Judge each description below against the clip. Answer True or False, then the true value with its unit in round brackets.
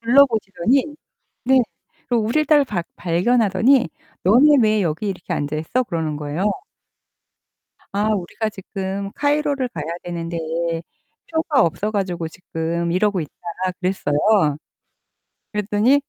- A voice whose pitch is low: False (205 Hz)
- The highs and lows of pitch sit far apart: True (6.4 semitones)